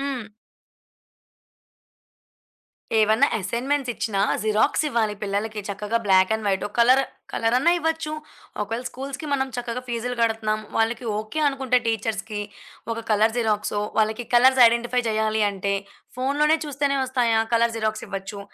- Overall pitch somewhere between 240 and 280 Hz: No, high, 230 Hz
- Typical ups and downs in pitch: Yes, average, 3.1 semitones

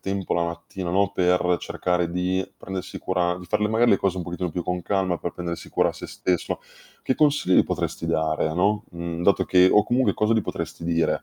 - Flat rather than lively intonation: Yes, narrow, 2.2 semitones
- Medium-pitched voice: No, very low, 90 Hz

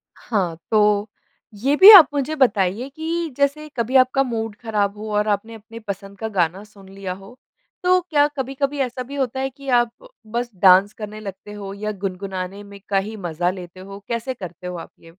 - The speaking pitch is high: Yes, high, 215 Hz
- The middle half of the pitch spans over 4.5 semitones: Yes, average, 5.0 semitones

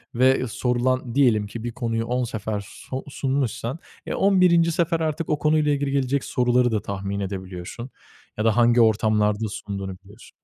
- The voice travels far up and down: No, average, 4.6 semitones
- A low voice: Yes, low, 120 Hz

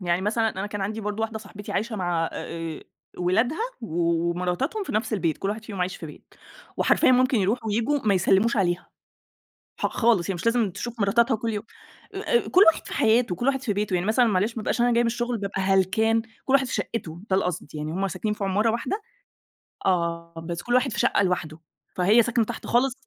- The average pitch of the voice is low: No, high, 210 Hz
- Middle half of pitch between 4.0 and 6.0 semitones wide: Yes, average, 4.4 semitones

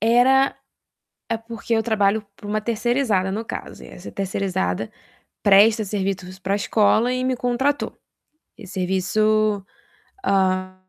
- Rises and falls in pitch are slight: No, average, 3.2 semitones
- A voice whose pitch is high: Yes, high, 210 Hz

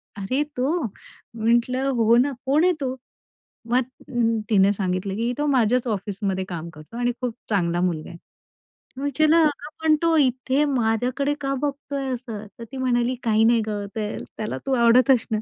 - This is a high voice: Yes, high, 240 Hz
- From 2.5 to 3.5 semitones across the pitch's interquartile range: No, average, 4.1 semitones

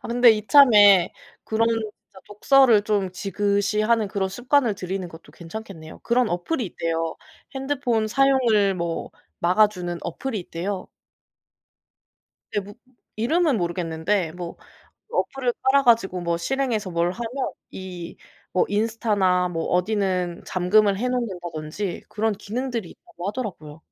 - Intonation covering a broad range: No, average, 4.5 semitones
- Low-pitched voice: No, high, 205 Hz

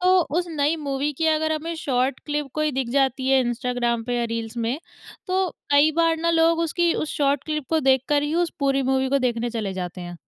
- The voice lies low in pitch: No, very high, 280 Hz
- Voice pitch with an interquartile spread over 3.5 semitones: Yes, average, 4.2 semitones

